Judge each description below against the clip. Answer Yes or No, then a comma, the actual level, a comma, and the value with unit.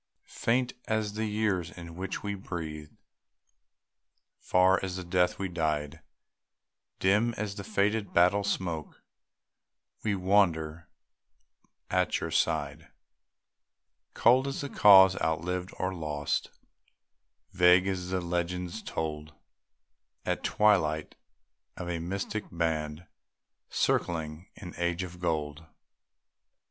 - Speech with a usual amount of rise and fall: Yes, average, 3.4 semitones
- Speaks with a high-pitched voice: No, very low, 90 Hz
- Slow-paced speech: Yes, slow, 110 wpm